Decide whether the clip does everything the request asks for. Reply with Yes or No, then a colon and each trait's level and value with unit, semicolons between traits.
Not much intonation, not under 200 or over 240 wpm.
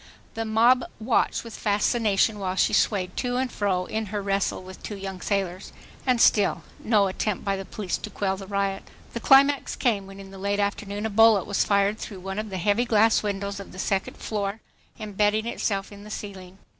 Yes: narrow, 2.0 semitones; fast, 205 wpm